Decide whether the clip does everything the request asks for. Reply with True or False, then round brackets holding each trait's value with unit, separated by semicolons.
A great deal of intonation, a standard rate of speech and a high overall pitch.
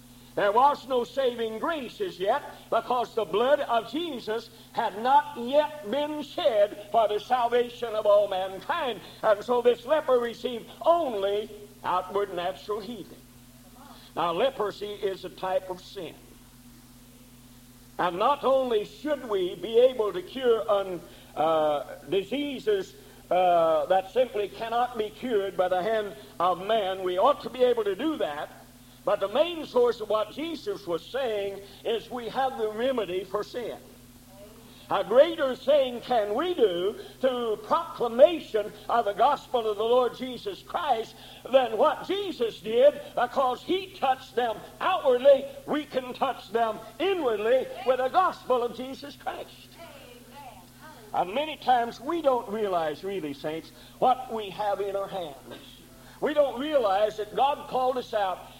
True (5.9 semitones; 145 wpm; 235 Hz)